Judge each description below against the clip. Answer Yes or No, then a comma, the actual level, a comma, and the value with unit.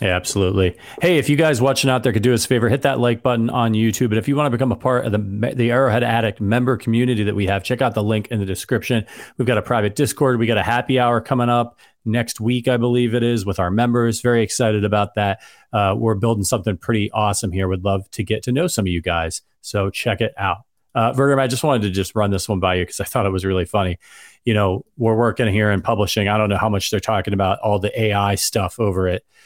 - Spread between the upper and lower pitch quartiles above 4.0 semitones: No, average, 3.3 semitones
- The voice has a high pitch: No, low, 110 Hz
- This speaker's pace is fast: Yes, fast, 265 wpm